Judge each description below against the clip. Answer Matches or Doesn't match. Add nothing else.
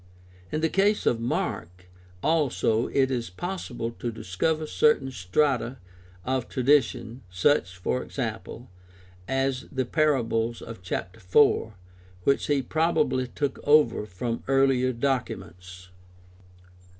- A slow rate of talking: Matches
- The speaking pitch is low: Matches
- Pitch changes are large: Doesn't match